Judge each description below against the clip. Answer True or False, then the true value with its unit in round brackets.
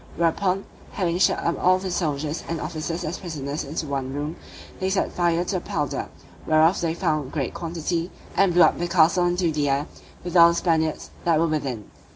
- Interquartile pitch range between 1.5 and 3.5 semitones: True (2.4 semitones)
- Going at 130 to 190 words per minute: False (200 wpm)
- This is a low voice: False (165 Hz)